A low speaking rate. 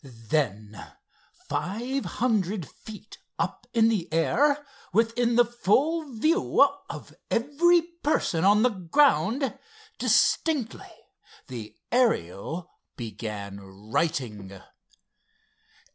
Yes: slow, 85 wpm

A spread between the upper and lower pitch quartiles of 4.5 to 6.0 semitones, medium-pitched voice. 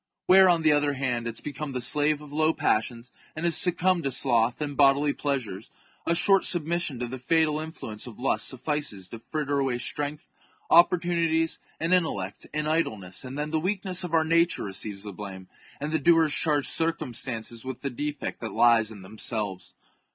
Yes: wide, 5.4 semitones; medium, 145 Hz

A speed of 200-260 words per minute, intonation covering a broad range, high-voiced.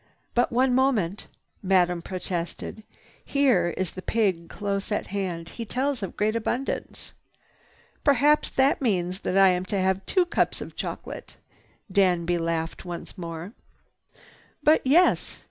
No: slow, 135 wpm; wide, 5.8 semitones; high, 195 Hz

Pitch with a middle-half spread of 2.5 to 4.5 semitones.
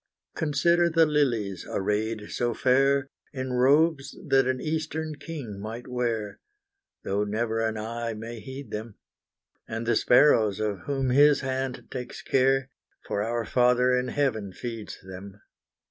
Yes: average, 3.9 semitones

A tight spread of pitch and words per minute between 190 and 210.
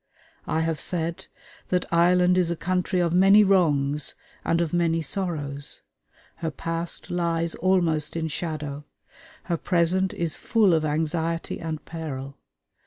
No: narrow, 2.1 semitones; slow, 135 wpm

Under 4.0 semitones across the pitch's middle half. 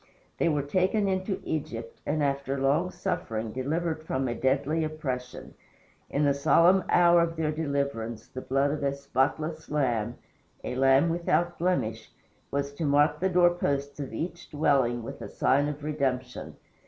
Yes: average, 3.6 semitones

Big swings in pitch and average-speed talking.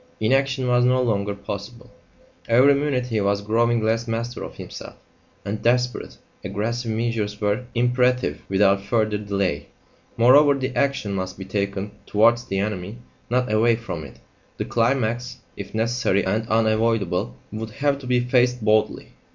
No: average, 3.3 semitones; average, 150 wpm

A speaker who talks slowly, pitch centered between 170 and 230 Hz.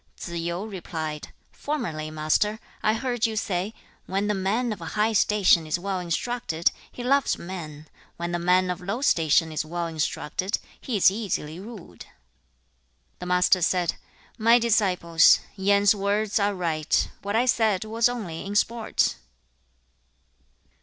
No: average, 150 wpm; high, 190 Hz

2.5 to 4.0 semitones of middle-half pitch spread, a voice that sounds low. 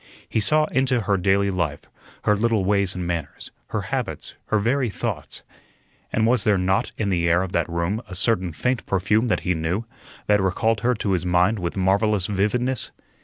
Yes: average, 3.5 semitones; low, 100 Hz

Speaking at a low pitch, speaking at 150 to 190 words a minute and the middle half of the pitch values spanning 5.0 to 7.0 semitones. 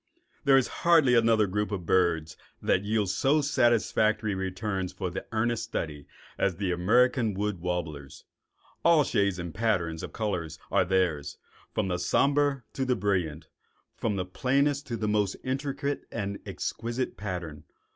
No: low, 105 Hz; average, 140 wpm; wide, 5.4 semitones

